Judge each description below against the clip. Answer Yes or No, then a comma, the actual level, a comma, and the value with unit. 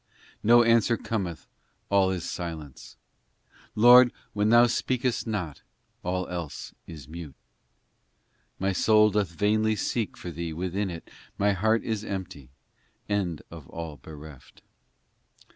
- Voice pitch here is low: Yes, very low, 95 Hz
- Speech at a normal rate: No, slow, 125 wpm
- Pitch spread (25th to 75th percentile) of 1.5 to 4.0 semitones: No, average, 4.7 semitones